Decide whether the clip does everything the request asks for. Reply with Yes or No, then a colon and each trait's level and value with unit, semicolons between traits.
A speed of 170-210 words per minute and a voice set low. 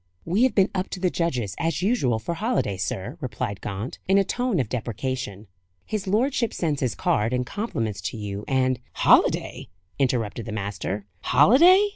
Yes: average, 175 wpm; low, 130 Hz